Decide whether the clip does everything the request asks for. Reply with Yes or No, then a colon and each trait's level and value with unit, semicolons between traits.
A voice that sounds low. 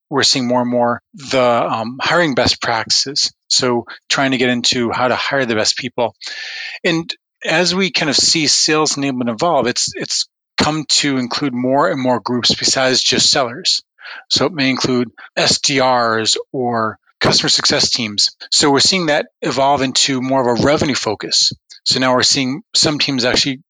Yes: low, 130 Hz